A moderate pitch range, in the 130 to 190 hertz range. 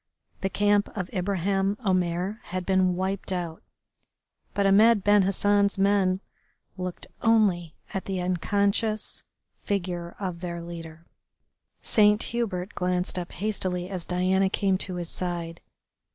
No: narrow, 2.1 semitones; medium, 185 Hz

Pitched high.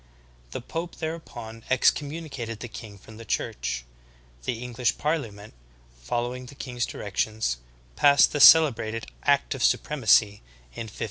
No: low, 120 Hz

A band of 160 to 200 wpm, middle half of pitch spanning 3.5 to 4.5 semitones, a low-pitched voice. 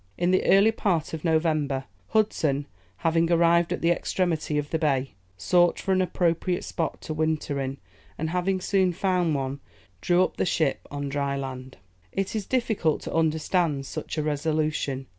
No: average, 170 wpm; average, 3.8 semitones; medium, 160 Hz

